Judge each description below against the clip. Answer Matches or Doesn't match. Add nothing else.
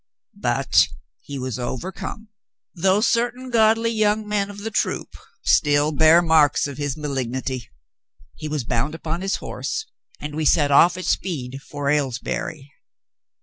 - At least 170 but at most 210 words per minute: Doesn't match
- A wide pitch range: Matches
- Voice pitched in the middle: Matches